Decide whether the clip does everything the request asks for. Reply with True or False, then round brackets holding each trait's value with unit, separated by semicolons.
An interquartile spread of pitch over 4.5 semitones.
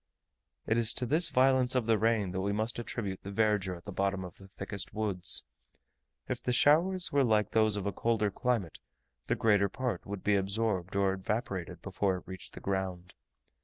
False (3.4 semitones)